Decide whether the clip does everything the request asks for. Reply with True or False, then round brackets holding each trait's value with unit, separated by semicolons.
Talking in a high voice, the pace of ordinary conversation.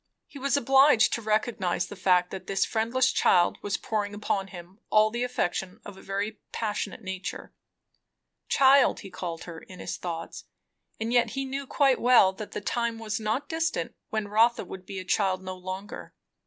True (210 Hz; 180 wpm)